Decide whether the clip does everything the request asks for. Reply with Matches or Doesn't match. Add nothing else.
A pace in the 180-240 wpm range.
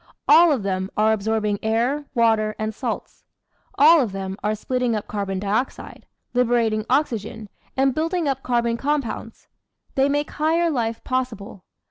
Doesn't match